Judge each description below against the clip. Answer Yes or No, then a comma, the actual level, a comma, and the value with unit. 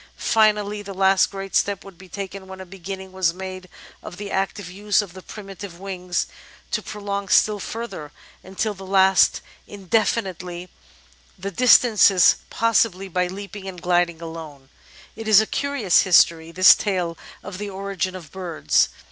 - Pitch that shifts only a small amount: Yes, narrow, 2.0 semitones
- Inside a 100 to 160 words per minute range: Yes, average, 155 wpm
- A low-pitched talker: No, high, 190 Hz